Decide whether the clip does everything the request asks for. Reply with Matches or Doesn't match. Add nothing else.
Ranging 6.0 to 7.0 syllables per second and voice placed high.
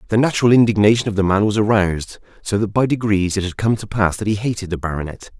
Doesn't match